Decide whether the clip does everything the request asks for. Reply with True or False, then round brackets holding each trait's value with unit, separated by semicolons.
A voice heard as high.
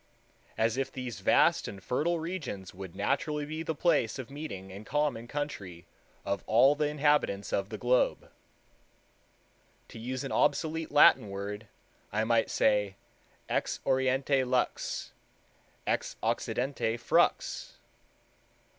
False (125 Hz)